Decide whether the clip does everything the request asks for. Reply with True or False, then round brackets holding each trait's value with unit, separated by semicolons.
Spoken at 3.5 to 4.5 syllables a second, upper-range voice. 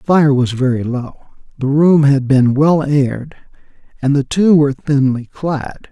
False (4.3 syllables/s; 140 Hz)